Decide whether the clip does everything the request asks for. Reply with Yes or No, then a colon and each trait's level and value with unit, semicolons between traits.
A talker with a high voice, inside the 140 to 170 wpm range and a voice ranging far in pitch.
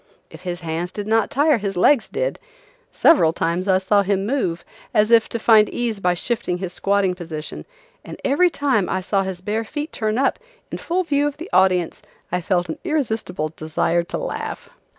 No: high, 200 Hz; average, 190 wpm; wide, 6.0 semitones